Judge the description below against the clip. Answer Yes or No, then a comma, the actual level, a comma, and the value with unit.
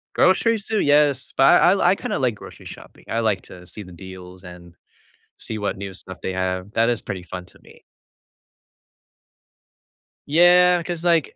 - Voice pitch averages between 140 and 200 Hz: No, low, 110 Hz